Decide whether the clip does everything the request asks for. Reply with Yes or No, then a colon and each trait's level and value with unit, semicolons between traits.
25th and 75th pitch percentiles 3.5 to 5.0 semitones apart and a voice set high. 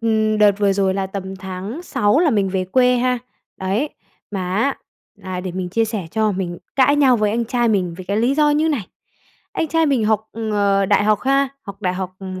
Yes: average, 4.4 semitones; high, 210 Hz